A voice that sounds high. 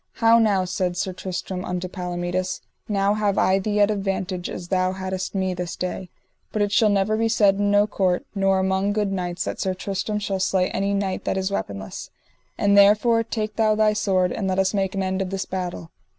Yes: high, 195 Hz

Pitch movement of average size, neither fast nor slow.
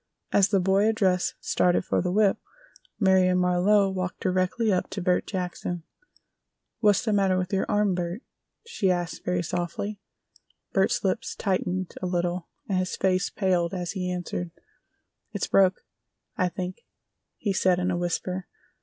No: narrow, 1.5 semitones; average, 155 wpm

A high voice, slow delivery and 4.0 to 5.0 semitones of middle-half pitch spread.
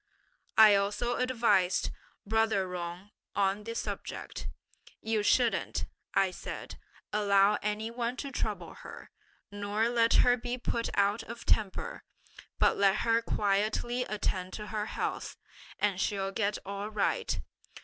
No: high, 210 Hz; slow, 130 wpm; narrow, 2.6 semitones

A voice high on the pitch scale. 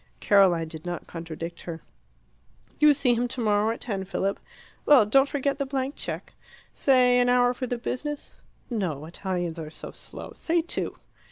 Yes: high, 230 Hz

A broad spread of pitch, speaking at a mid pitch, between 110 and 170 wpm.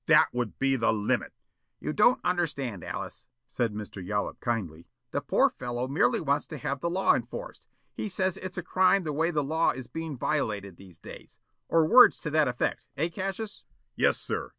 No: wide, 6.7 semitones; medium, 145 Hz; average, 190 wpm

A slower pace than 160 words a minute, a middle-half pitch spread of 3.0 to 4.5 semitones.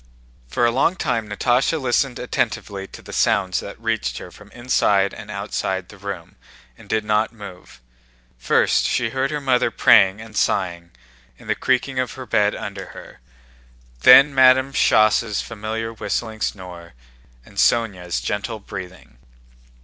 Yes: average, 150 wpm; average, 3.8 semitones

